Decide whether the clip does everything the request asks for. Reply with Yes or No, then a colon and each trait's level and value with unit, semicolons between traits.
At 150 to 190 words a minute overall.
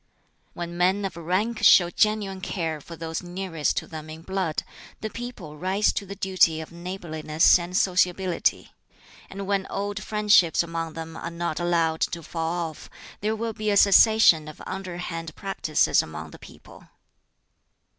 Yes: average, 155 wpm